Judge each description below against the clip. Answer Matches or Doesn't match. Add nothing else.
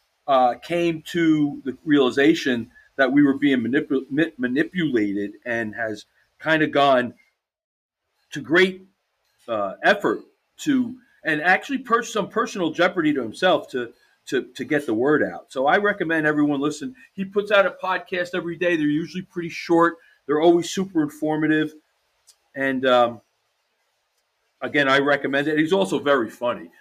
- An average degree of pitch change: Matches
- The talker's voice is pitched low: Doesn't match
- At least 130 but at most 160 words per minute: Matches